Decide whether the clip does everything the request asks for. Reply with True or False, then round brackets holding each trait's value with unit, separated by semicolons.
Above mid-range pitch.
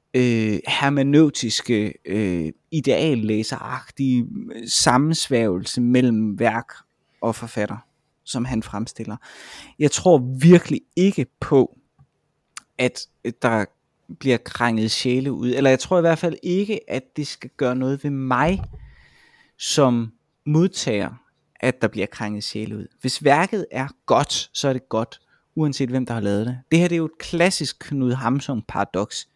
False (130 Hz)